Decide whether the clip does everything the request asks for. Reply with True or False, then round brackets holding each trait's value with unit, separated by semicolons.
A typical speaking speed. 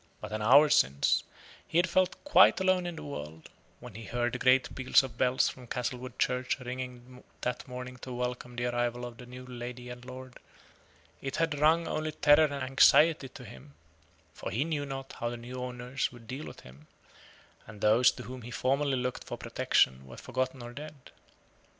True (195 wpm)